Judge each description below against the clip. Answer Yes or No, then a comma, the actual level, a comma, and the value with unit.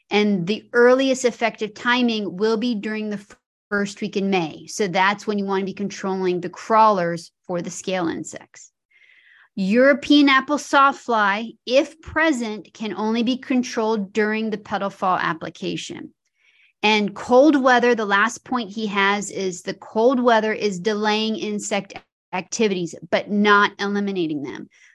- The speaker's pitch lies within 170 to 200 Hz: No, high, 215 Hz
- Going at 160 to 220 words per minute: No, average, 150 wpm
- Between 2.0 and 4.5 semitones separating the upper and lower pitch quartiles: Yes, average, 3.6 semitones